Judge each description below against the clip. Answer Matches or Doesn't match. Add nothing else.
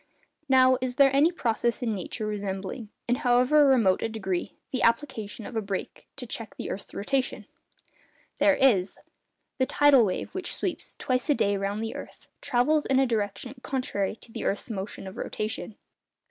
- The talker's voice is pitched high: Matches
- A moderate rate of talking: Matches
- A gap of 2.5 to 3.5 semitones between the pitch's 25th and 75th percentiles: Doesn't match